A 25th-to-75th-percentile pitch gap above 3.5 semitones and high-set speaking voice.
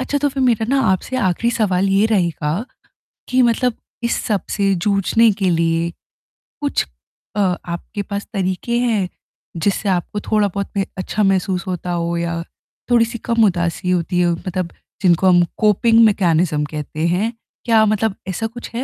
Yes: average, 4.1 semitones; high, 195 Hz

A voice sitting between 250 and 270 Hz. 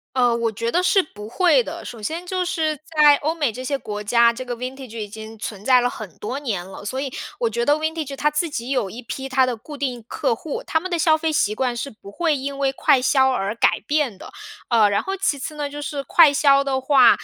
Yes: very high, 265 Hz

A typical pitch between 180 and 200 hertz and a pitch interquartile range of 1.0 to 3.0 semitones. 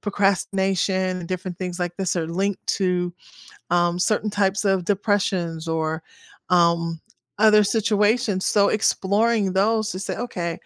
Yes: high, 190 Hz; average, 2.7 semitones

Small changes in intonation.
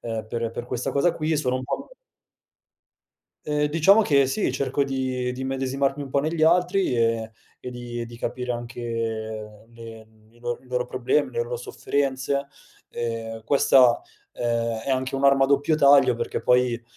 No: average, 3.1 semitones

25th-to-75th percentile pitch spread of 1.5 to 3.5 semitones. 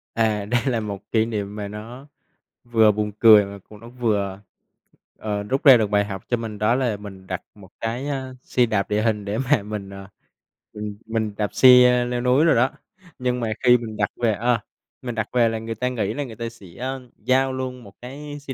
Yes: average, 3.1 semitones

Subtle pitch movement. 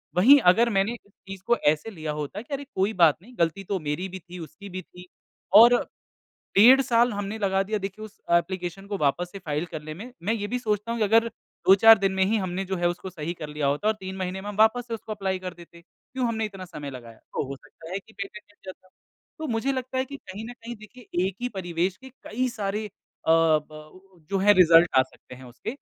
No: average, 4.2 semitones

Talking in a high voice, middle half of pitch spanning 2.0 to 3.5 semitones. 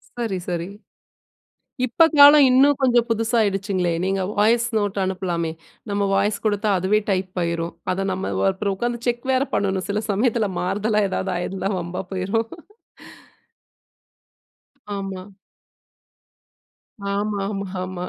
Yes: high, 200 Hz; average, 3.2 semitones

